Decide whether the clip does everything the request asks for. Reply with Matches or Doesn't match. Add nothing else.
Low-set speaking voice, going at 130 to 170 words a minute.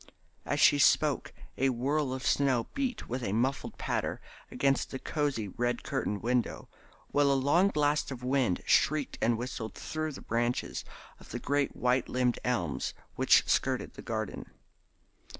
Matches